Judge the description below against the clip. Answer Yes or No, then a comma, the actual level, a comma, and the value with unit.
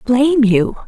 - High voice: Yes, high, 245 Hz